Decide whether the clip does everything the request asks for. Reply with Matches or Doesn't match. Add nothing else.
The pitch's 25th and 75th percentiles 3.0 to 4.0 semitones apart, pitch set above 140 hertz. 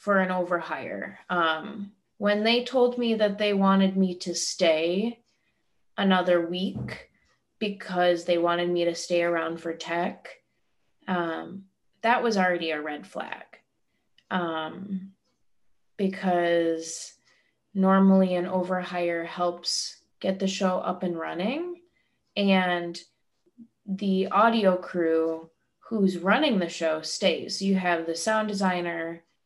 Doesn't match